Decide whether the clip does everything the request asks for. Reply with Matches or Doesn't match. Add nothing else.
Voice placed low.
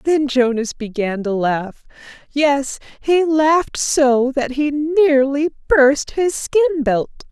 Doesn't match